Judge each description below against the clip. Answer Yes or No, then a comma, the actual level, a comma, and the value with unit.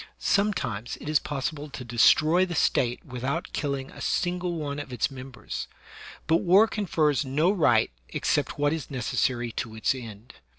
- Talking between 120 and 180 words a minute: Yes, average, 170 wpm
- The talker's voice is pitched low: No, medium, 145 Hz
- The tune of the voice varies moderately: Yes, average, 4.5 semitones